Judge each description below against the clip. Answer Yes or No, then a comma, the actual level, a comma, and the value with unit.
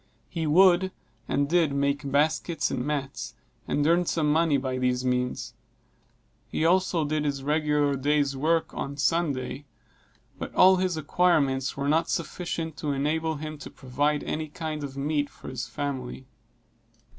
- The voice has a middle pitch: Yes, medium, 150 Hz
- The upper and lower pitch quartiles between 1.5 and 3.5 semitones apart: Yes, narrow, 2.6 semitones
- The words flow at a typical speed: Yes, average, 150 wpm